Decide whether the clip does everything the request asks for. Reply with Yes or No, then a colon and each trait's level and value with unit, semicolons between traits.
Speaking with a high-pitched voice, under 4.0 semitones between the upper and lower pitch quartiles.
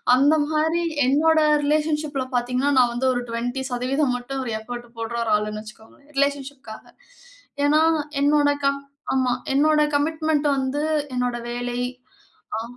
Yes: very high, 270 Hz; average, 3.4 semitones